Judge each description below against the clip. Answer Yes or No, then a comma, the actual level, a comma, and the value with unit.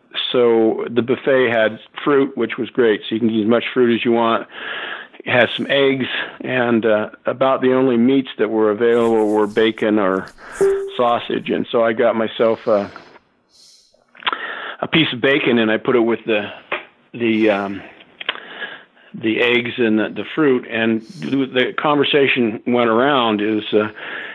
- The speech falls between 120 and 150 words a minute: No, average, 165 wpm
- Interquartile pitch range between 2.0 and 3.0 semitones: Yes, average, 2.7 semitones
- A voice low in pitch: Yes, low, 115 Hz